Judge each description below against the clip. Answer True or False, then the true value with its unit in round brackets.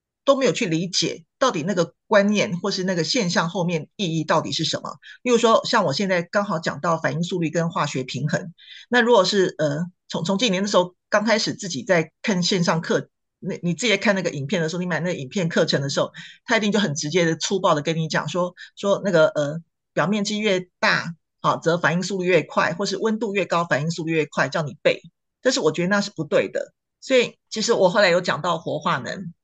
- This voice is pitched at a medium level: True (180 Hz)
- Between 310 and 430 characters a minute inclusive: True (330 characters per minute)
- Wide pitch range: False (3.7 semitones)